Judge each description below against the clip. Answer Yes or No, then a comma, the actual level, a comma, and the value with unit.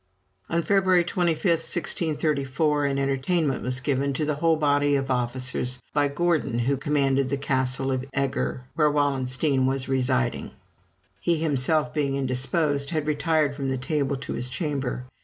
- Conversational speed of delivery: Yes, average, 150 wpm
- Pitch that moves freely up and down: No, narrow, 2.6 semitones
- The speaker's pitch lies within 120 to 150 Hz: Yes, medium, 140 Hz